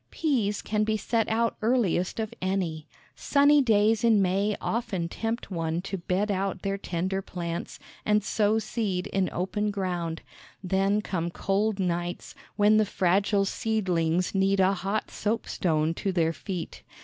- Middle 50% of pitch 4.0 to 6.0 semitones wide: No, average, 3.1 semitones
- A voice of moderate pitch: No, high, 195 Hz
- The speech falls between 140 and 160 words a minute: Yes, average, 150 wpm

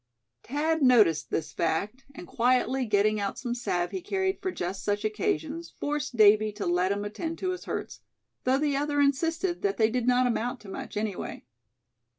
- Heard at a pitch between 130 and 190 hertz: No, high, 245 Hz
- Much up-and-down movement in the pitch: Yes, wide, 6.2 semitones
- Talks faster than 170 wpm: Yes, average, 180 wpm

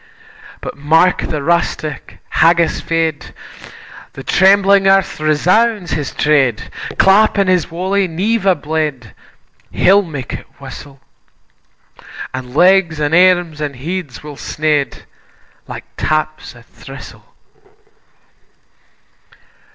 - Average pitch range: Yes, average, 4.1 semitones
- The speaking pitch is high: No, medium, 160 Hz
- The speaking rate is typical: No, slow, 105 wpm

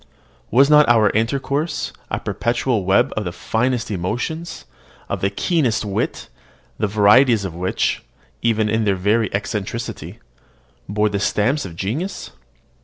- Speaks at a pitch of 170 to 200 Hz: No, low, 110 Hz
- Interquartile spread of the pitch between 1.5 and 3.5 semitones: No, average, 4.1 semitones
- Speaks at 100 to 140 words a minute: Yes, slow, 135 wpm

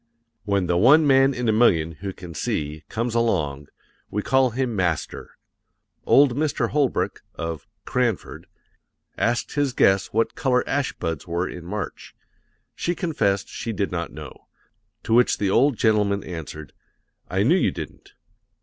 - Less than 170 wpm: Yes, average, 150 wpm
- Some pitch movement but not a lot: No, wide, 6.4 semitones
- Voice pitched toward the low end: Yes, low, 105 Hz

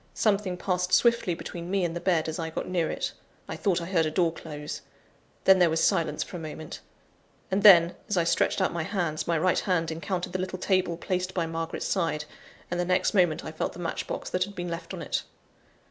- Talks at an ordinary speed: No, fast, 230 wpm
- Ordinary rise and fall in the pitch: No, narrow, 2.1 semitones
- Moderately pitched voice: Yes, medium, 175 Hz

